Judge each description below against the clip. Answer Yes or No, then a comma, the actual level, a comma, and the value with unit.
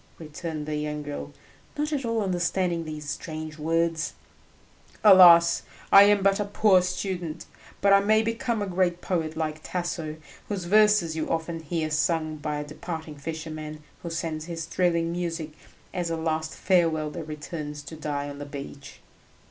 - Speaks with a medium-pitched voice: Yes, medium, 165 Hz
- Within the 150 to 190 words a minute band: Yes, average, 165 wpm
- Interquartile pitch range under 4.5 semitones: Yes, average, 2.9 semitones